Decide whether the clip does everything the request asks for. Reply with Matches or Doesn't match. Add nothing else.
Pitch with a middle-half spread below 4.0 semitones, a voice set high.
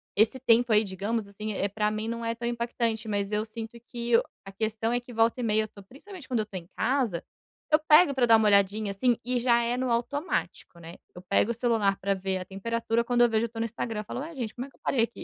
Matches